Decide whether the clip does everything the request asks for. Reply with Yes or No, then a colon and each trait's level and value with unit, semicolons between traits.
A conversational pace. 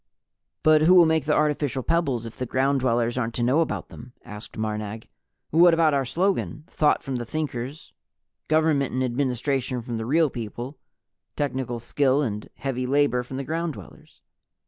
Yes: average, 170 wpm